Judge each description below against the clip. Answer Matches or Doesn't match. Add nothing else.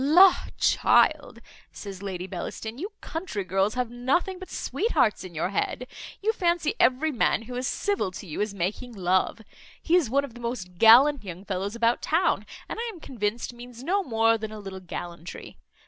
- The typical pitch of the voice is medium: Doesn't match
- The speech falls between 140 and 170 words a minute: Doesn't match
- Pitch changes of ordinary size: Doesn't match